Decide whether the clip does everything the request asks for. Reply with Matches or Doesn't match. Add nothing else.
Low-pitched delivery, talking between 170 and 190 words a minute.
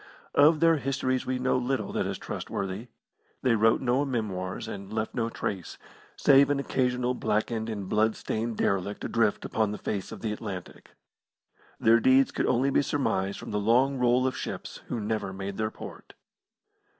Matches